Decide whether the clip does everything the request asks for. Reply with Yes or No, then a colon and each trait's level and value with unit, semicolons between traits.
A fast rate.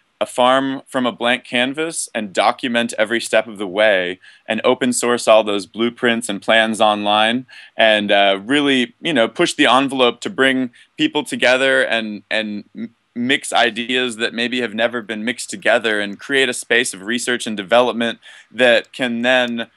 No: average, 175 wpm